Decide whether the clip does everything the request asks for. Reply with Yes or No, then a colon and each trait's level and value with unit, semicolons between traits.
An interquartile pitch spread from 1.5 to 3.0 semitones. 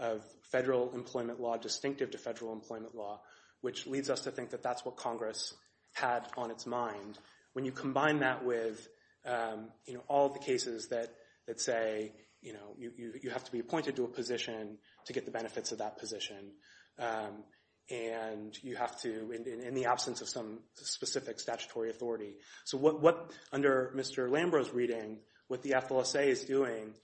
Yes: narrow, 2.6 semitones